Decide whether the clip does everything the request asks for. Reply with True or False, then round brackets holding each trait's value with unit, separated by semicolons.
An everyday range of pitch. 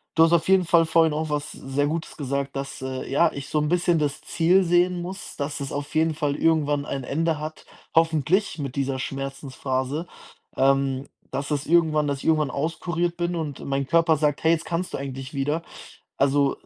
True (3.1 semitones)